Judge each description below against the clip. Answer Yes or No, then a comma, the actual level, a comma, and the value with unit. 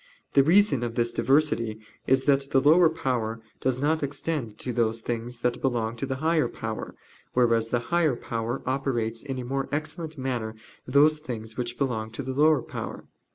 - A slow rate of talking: No, average, 180 wpm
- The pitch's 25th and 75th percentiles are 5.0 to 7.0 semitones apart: No, average, 3.8 semitones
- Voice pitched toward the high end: No, low, 130 Hz